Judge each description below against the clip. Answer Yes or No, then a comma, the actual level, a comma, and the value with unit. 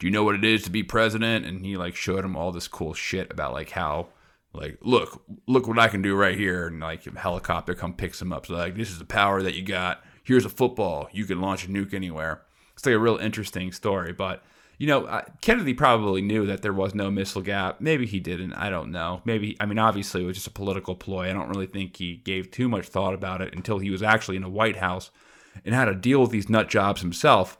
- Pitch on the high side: No, very low, 95 Hz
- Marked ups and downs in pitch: No, average, 2.9 semitones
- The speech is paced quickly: Yes, fast, 255 wpm